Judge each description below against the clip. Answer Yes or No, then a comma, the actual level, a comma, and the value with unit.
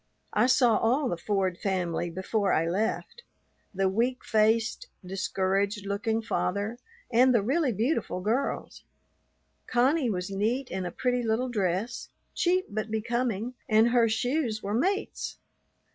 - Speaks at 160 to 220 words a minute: No, slow, 135 wpm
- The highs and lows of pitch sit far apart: No, average, 4.0 semitones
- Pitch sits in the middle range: No, high, 220 Hz